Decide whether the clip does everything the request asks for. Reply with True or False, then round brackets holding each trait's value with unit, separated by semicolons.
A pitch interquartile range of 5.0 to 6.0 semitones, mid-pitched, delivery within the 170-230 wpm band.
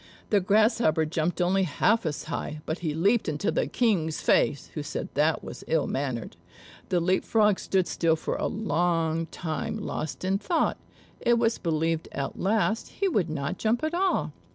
True (5.5 semitones; 175 Hz; 175 wpm)